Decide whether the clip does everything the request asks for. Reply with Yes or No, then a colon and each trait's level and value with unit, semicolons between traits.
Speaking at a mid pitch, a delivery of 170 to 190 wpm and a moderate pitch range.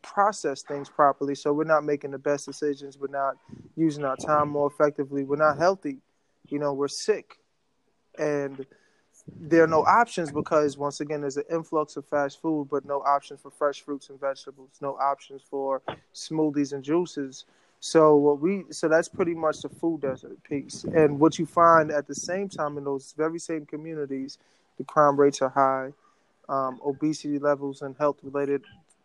No: medium, 145 Hz; average, 180 wpm; narrow, 2.0 semitones